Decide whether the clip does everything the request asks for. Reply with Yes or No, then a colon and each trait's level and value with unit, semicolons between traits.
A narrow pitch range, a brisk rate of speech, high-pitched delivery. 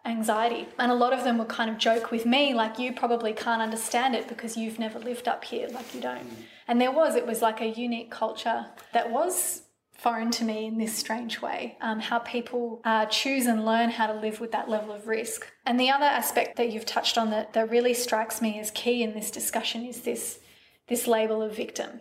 Yes: narrow, 1.5 semitones; fast, 230 wpm; high, 230 Hz